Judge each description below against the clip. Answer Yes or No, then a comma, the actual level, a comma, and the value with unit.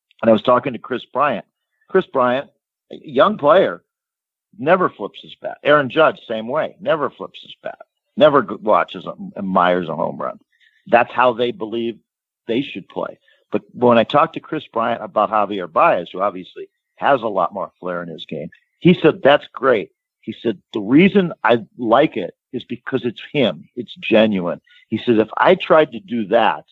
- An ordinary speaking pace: Yes, average, 185 wpm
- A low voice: Yes, low, 130 Hz